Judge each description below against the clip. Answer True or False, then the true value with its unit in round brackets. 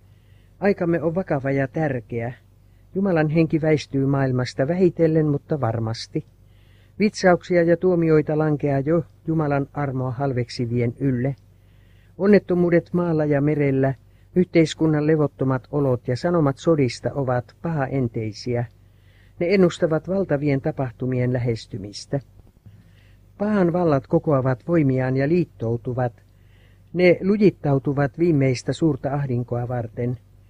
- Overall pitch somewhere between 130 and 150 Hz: True (135 Hz)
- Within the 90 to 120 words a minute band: True (100 wpm)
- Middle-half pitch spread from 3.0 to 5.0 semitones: False (5.6 semitones)